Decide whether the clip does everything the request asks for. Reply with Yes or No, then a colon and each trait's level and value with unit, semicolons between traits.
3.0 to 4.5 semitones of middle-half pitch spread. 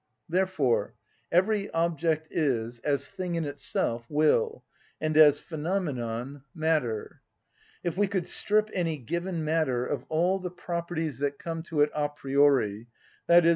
Yes: average, 3.6 semitones